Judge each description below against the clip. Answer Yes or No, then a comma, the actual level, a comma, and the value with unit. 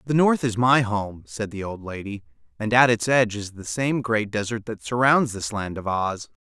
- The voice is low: Yes, low, 110 Hz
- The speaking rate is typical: No, fast, 225 wpm